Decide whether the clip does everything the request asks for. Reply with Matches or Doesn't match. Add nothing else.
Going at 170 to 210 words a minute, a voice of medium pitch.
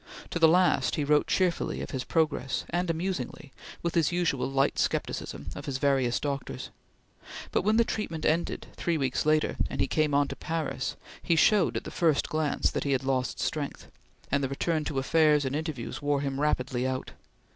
Matches